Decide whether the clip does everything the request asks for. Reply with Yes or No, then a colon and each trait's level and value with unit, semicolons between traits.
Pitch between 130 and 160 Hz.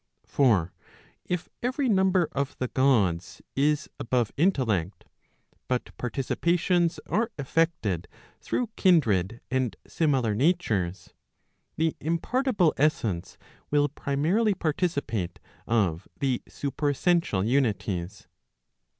Yes: medium, 140 Hz